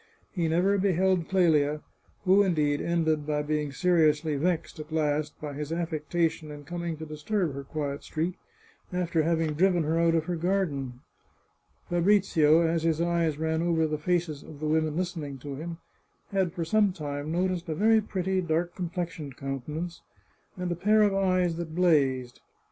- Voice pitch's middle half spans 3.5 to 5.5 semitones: No, average, 2.8 semitones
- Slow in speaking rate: No, average, 170 wpm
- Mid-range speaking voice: Yes, medium, 165 Hz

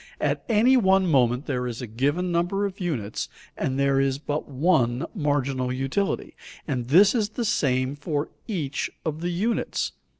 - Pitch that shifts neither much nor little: No, wide, 5.9 semitones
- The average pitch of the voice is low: No, medium, 145 Hz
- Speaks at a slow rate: No, average, 165 wpm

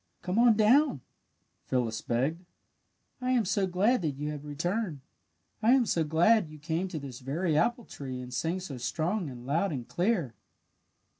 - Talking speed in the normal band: Yes, average, 175 wpm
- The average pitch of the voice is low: No, medium, 165 Hz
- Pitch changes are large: Yes, wide, 6.8 semitones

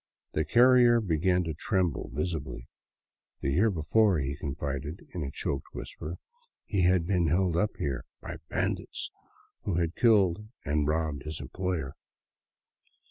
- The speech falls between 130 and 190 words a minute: Yes, slow, 135 wpm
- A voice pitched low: Yes, very low, 85 Hz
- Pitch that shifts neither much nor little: Yes, average, 4.3 semitones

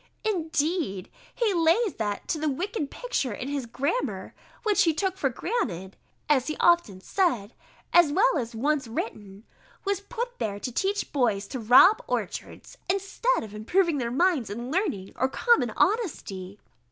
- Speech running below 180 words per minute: Yes, average, 160 wpm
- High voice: Yes, very high, 300 Hz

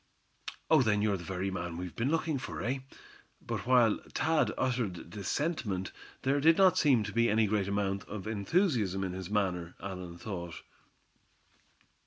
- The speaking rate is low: No, average, 165 wpm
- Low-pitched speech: Yes, low, 105 Hz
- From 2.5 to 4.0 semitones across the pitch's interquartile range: No, average, 5.3 semitones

